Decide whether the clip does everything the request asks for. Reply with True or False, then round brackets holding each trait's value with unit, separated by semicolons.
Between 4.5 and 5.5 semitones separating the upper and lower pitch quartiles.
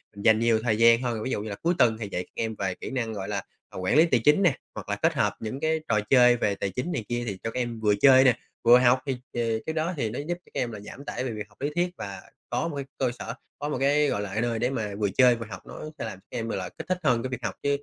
False (3.8 semitones)